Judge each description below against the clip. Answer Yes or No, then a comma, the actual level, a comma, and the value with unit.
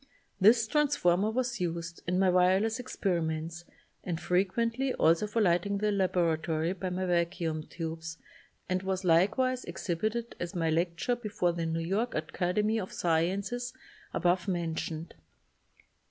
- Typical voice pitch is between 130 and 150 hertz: No, medium, 180 Hz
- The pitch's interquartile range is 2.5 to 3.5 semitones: No, average, 4.0 semitones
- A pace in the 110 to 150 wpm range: Yes, slow, 135 wpm